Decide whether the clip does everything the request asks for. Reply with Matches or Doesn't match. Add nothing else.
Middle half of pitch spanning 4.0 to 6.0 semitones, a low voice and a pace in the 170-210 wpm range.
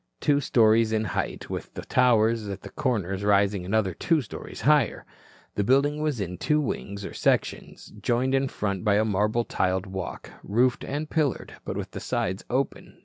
Matches